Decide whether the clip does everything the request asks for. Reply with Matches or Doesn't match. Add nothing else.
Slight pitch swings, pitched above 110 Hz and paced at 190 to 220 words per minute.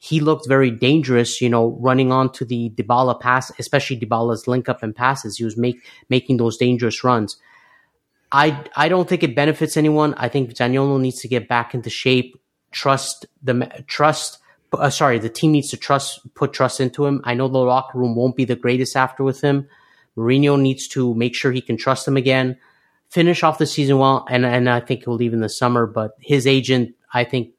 Matches